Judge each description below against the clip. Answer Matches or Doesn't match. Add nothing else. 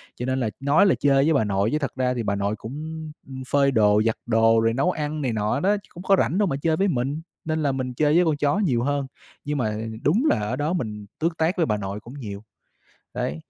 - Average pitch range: Doesn't match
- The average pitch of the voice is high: Doesn't match